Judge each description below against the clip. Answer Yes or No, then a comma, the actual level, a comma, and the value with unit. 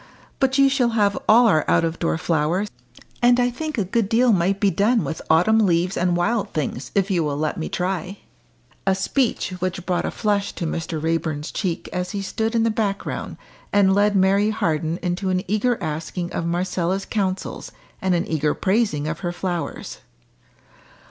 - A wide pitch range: No, average, 4.0 semitones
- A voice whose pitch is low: No, high, 190 Hz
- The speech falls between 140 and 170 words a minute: No, average, 185 wpm